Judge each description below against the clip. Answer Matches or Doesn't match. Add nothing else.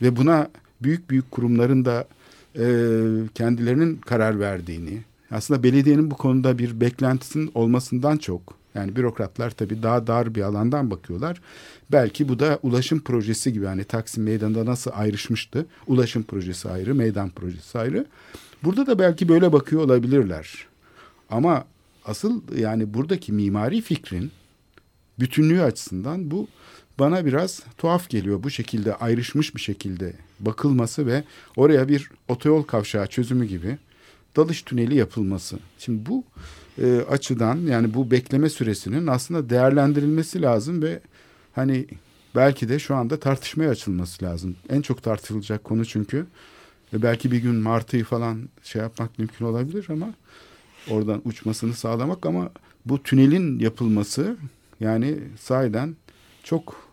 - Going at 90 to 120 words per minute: Doesn't match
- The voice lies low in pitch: Matches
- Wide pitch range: Doesn't match